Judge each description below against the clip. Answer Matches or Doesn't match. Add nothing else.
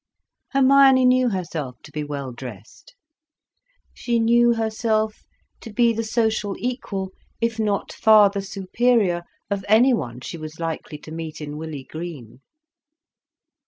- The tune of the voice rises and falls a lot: Matches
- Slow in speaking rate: Matches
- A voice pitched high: Matches